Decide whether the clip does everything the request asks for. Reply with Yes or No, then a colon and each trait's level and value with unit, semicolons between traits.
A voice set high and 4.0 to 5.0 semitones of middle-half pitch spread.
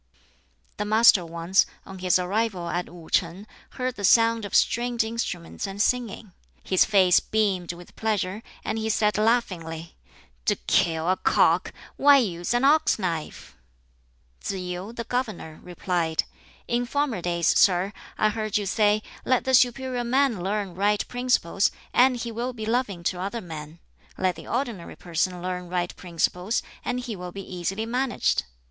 Yes: high, 200 Hz; average, 4.6 semitones